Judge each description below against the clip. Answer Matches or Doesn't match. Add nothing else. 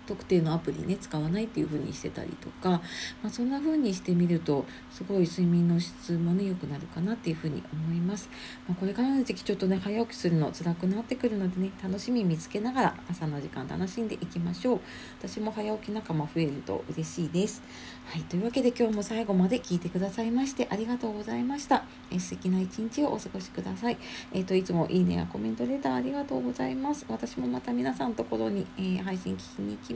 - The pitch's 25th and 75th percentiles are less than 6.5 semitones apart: Matches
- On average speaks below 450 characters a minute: Doesn't match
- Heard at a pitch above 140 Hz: Matches